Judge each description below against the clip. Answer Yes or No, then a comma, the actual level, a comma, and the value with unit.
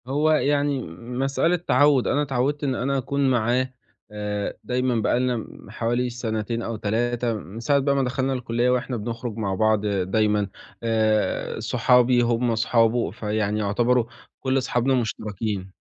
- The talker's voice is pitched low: Yes, low, 120 Hz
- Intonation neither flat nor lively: Yes, average, 3.1 semitones